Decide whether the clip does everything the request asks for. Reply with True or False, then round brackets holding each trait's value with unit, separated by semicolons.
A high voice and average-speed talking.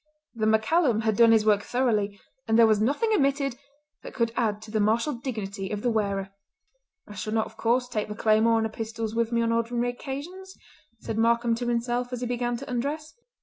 False (230 Hz; 210 wpm)